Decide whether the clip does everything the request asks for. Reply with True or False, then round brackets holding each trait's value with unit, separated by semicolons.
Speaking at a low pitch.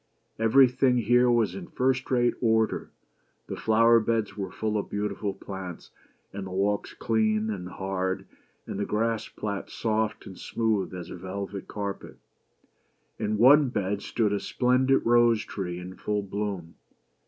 True (105 Hz)